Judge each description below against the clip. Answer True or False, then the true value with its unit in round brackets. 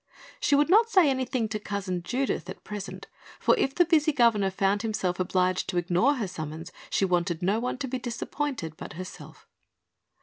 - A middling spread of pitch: False (6.7 semitones)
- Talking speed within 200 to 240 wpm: False (180 wpm)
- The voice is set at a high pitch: True (210 Hz)